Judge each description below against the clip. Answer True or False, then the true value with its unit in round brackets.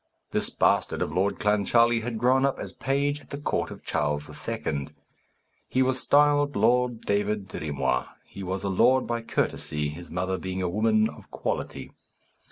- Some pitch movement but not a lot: False (5.7 semitones)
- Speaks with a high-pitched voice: False (110 Hz)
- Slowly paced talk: False (175 wpm)